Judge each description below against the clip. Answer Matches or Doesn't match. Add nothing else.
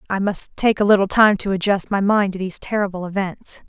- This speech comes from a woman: Matches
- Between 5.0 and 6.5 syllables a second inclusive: Matches